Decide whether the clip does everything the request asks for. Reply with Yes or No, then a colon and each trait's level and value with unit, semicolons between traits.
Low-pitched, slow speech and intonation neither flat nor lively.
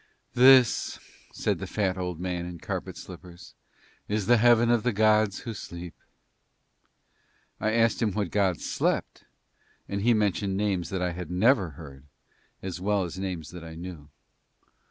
No: very low, 95 Hz; average, 155 wpm; average, 3.5 semitones